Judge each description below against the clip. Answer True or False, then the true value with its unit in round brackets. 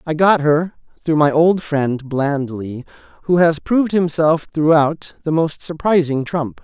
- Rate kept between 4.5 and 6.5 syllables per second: False (4.0 syllables/s)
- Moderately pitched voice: True (155 Hz)